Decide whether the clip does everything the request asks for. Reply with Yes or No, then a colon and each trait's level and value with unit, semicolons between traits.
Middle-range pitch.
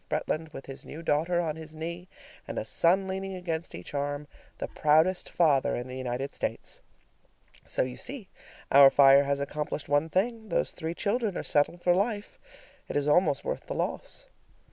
Yes: medium, 160 Hz